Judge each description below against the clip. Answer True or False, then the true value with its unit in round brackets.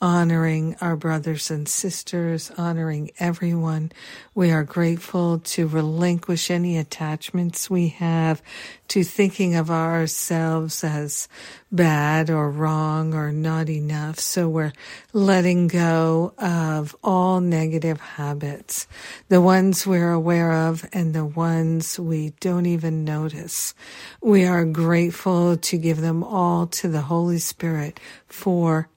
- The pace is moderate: False (120 wpm)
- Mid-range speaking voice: True (165 Hz)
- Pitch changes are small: True (1.8 semitones)